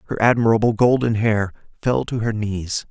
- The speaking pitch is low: Yes, low, 110 Hz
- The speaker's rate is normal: Yes, average, 165 wpm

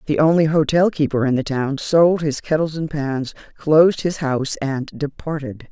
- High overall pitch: No, medium, 150 Hz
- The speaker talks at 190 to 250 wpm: No, average, 180 wpm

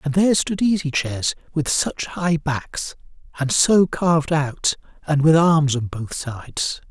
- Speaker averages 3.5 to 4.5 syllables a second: Yes, 4.0 syllables/s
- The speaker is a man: Yes, male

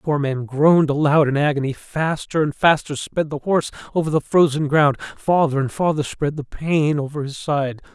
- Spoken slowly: No, average, 190 wpm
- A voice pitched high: No, medium, 150 Hz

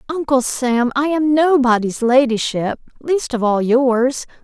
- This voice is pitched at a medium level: No, very high, 260 Hz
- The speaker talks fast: No, slow, 135 wpm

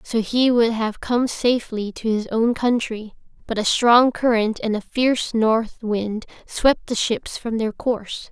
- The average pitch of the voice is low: No, high, 230 Hz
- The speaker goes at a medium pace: Yes, average, 180 wpm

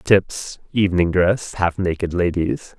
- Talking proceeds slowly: Yes, slow, 110 wpm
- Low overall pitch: Yes, very low, 90 Hz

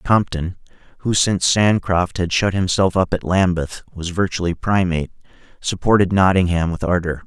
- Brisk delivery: No, average, 140 wpm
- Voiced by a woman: No, male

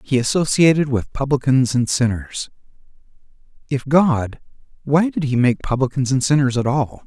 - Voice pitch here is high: No, low, 135 Hz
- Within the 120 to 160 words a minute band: Yes, average, 145 wpm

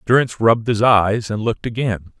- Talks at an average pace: Yes, average, 190 wpm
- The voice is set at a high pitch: No, low, 110 Hz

